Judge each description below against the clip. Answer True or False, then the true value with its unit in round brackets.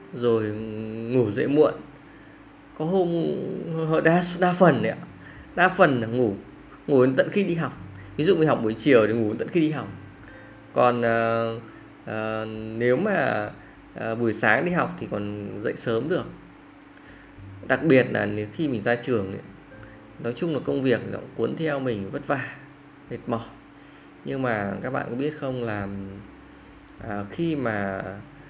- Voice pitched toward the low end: True (115 Hz)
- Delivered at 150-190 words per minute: True (170 wpm)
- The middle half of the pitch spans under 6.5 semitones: True (5.6 semitones)